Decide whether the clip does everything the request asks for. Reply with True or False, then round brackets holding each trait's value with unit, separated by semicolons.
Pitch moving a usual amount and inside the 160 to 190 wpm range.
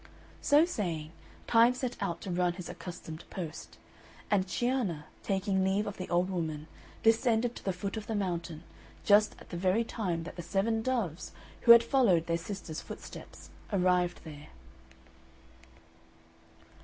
False (4.6 semitones; 150 wpm)